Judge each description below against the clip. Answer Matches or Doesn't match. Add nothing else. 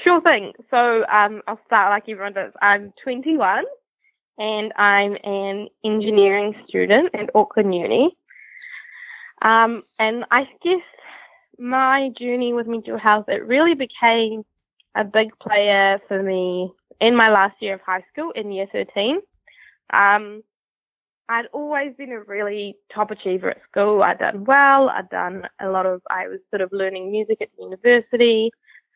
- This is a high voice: Matches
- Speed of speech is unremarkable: Matches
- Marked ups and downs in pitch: Doesn't match